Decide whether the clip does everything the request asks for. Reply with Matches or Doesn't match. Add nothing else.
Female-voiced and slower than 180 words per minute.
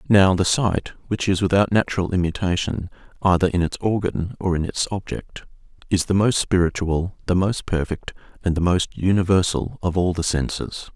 Doesn't match